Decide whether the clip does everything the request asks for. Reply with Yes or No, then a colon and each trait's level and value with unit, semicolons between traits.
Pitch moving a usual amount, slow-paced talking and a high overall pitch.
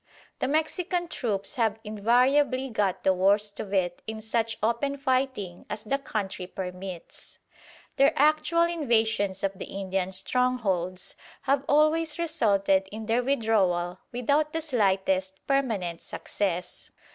No: wide, 6.2 semitones; slow, 125 wpm; high, 220 Hz